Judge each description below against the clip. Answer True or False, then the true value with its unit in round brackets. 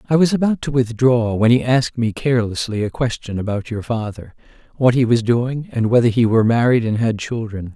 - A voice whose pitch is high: False (120 Hz)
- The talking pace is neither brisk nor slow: False (210 wpm)